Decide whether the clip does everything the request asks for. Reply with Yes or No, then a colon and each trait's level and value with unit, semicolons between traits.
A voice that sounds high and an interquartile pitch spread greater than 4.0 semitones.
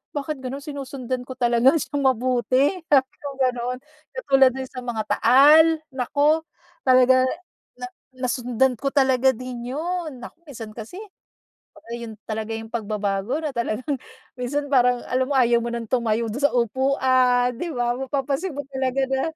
No: very high, 255 Hz; narrow, 2.5 semitones